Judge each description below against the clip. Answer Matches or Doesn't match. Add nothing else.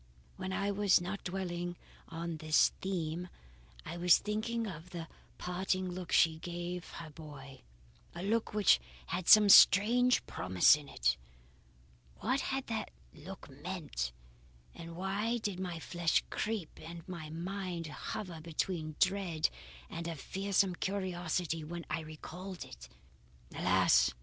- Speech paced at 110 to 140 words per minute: Matches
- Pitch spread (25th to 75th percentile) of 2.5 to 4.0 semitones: Matches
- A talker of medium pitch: Matches